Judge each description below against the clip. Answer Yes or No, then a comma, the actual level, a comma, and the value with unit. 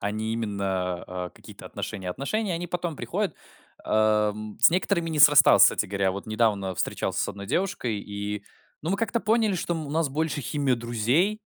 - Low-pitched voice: Yes, low, 120 Hz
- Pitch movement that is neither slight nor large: No, wide, 8.7 semitones